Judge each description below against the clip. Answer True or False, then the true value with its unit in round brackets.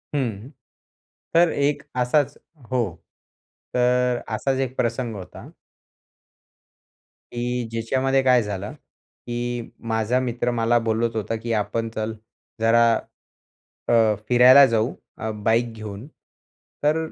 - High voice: False (120 Hz)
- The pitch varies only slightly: True (2.3 semitones)